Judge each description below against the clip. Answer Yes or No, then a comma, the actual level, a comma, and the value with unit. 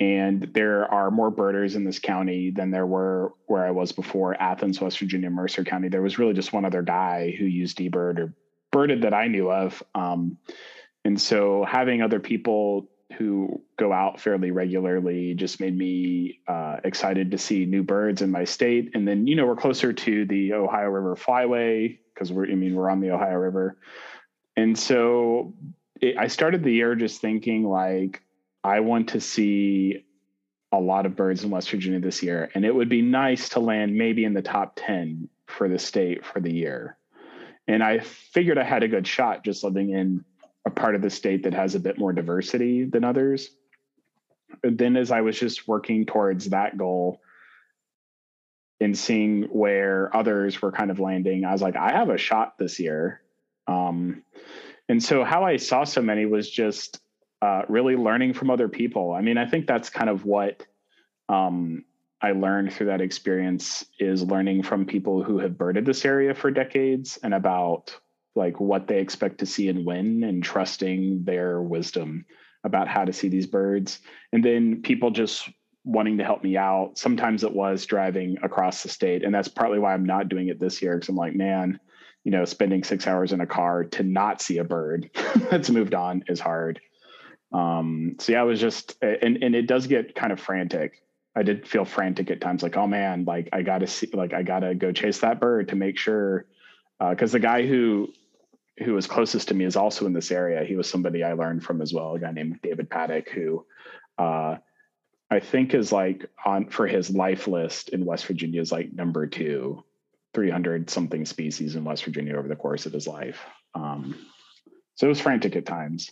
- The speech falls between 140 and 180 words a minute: No, average, 195 wpm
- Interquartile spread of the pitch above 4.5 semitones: No, average, 3.3 semitones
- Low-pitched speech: Yes, very low, 95 Hz